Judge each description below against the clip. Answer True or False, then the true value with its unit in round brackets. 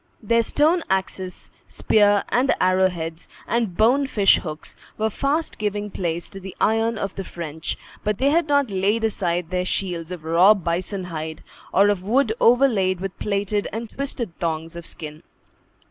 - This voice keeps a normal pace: True (165 wpm)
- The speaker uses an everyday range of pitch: True (4.3 semitones)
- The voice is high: True (195 Hz)